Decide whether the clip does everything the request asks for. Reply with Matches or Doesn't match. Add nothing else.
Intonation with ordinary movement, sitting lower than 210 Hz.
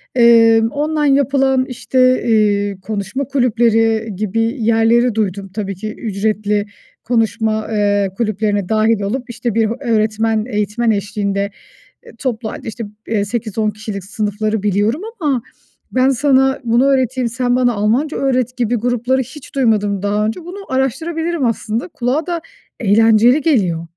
Doesn't match